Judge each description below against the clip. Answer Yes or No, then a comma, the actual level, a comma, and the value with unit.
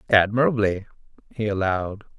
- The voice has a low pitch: Yes, low, 105 Hz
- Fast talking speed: No, slow, 80 wpm